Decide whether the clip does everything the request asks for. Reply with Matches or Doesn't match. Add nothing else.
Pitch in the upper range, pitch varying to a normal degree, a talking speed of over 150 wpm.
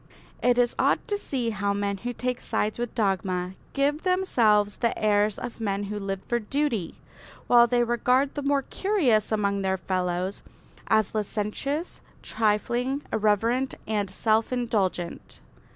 Doesn't match